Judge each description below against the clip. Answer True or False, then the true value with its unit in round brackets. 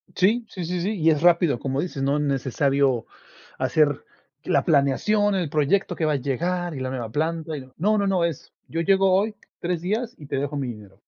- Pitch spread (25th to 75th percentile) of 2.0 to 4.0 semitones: False (4.8 semitones)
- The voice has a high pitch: False (155 Hz)